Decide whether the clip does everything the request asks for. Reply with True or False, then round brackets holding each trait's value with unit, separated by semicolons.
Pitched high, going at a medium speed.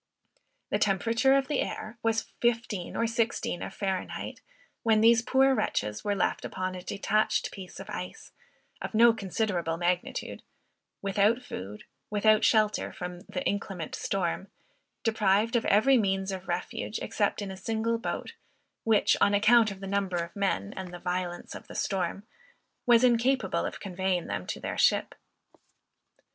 True (200 Hz; 155 wpm)